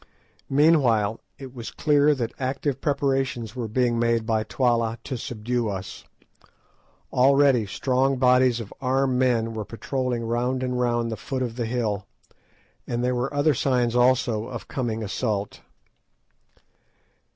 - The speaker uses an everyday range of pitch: No, narrow, 2.3 semitones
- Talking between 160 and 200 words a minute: No, average, 140 wpm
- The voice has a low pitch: Yes, low, 125 Hz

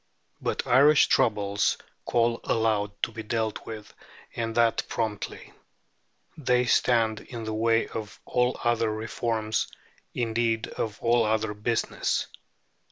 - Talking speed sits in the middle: No, slow, 120 wpm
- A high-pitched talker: No, low, 115 Hz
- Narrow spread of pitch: Yes, narrow, 1.4 semitones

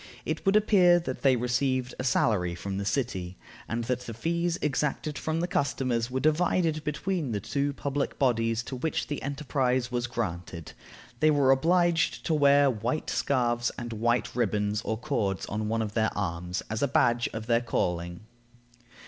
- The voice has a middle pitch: No, low, 125 Hz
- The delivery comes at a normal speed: Yes, average, 175 wpm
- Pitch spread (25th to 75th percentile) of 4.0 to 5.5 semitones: Yes, average, 4.6 semitones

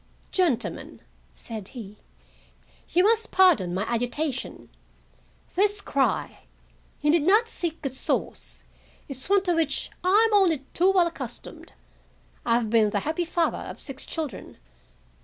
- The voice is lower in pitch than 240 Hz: No, very high, 315 Hz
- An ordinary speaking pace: No, slow, 130 wpm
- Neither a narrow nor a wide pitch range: No, wide, 7.3 semitones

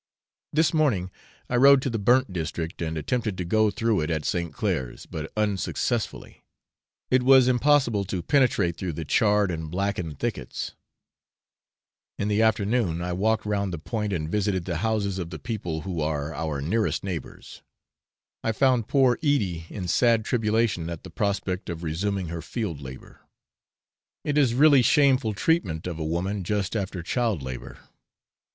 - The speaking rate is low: No, average, 160 wpm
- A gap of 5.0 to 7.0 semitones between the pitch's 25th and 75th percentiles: Yes, wide, 5.4 semitones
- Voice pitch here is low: Yes, low, 100 Hz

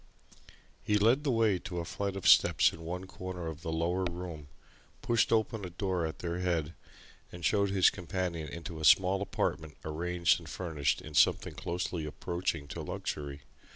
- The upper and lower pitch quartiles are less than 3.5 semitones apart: Yes, average, 2.7 semitones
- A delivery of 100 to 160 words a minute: No, average, 175 wpm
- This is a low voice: Yes, very low, 90 Hz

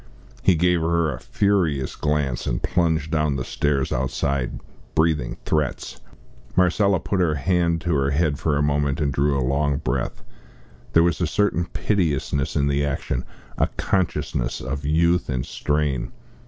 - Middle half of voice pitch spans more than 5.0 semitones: No, average, 3.4 semitones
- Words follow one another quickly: No, average, 155 wpm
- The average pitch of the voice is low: Yes, very low, 75 Hz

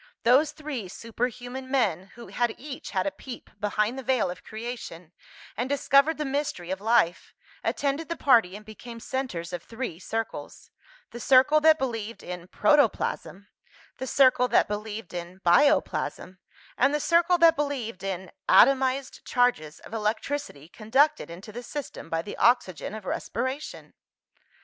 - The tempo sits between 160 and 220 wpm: No, average, 150 wpm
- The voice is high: Yes, high, 240 Hz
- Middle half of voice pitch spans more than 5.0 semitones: Yes, wide, 5.4 semitones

